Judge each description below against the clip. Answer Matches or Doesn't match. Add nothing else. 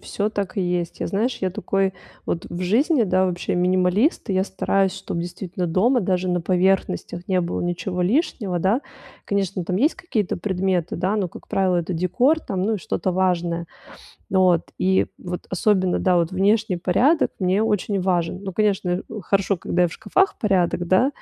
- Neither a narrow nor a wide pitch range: Doesn't match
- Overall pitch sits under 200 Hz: Matches